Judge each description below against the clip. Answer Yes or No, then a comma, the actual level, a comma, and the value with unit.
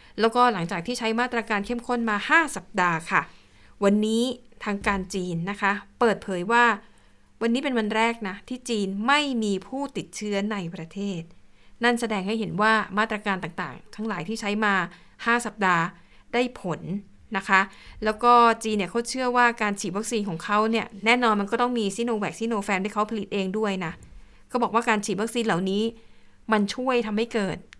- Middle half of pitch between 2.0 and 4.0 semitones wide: Yes, average, 2.9 semitones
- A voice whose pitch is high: Yes, high, 215 Hz